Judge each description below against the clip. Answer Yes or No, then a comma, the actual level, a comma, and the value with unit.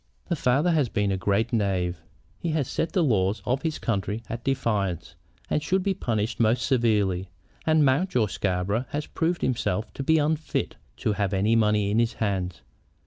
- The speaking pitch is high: No, low, 115 Hz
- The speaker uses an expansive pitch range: Yes, wide, 6.4 semitones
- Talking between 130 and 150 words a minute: No, average, 180 wpm